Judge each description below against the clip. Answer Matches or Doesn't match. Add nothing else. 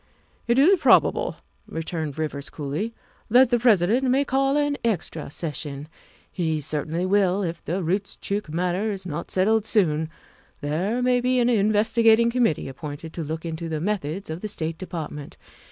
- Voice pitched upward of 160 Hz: Matches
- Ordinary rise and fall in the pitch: Doesn't match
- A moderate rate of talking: Matches